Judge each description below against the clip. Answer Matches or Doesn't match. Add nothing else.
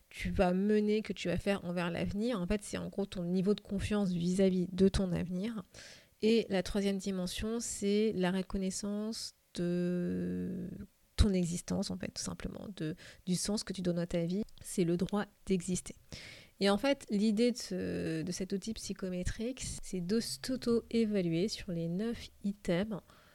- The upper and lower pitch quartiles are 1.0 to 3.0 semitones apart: Matches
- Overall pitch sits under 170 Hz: Doesn't match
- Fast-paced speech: Doesn't match